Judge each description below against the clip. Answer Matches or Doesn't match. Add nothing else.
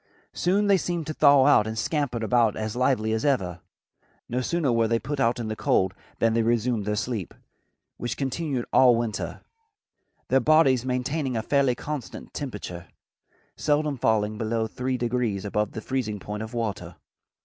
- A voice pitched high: Doesn't match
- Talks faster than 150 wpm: Matches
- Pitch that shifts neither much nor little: Matches